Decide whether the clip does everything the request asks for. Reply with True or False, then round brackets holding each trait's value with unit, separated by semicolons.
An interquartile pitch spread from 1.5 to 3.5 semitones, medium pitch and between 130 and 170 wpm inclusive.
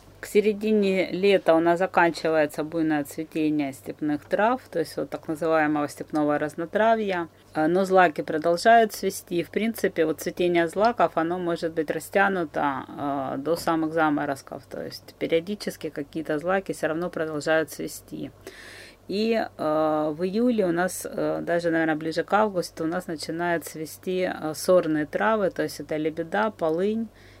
True (3.2 semitones; 165 Hz; 140 wpm)